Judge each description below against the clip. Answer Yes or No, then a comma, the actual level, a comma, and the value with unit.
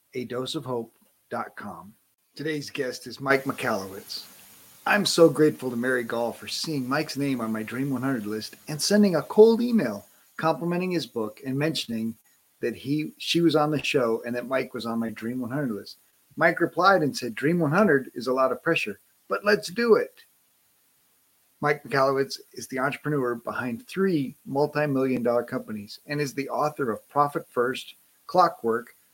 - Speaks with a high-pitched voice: No, medium, 140 Hz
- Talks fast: No, average, 175 wpm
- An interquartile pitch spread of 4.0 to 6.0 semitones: Yes, average, 4.6 semitones